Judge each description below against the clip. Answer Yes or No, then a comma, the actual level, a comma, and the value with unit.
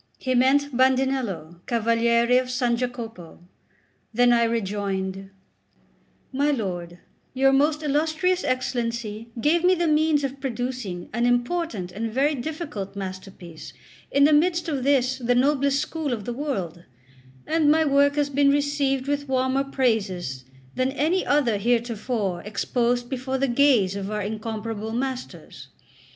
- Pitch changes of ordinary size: Yes, average, 4.6 semitones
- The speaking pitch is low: No, very high, 250 Hz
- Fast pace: No, average, 140 wpm